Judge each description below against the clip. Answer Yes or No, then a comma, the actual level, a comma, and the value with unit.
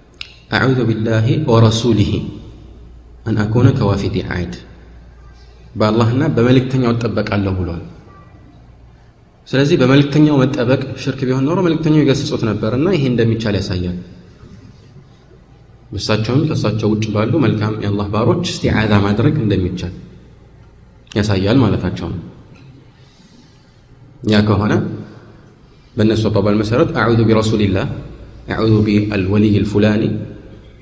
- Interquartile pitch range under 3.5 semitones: No, average, 4.1 semitones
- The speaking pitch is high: No, low, 110 Hz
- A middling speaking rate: No, fast, 120 wpm